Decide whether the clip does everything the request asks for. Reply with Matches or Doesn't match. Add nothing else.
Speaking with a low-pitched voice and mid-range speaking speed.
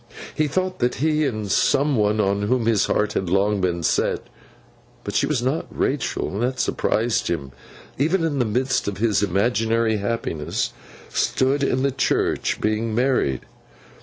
Matches